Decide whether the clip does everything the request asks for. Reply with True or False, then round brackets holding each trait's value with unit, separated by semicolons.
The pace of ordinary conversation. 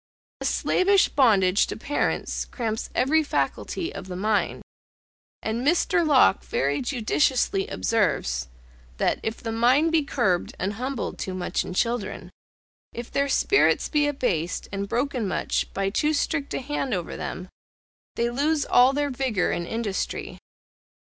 True (145 wpm)